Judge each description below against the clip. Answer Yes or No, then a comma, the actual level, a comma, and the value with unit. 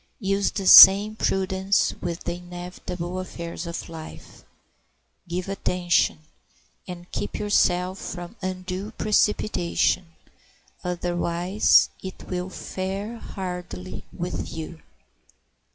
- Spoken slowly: Yes, slow, 95 wpm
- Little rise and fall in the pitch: Yes, narrow, 1.8 semitones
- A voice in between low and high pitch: Yes, medium, 180 Hz